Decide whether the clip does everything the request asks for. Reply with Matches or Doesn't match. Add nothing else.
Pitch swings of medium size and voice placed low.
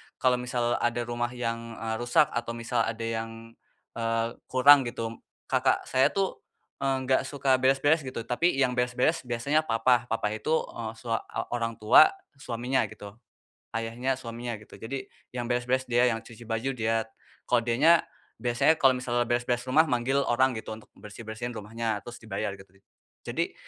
Doesn't match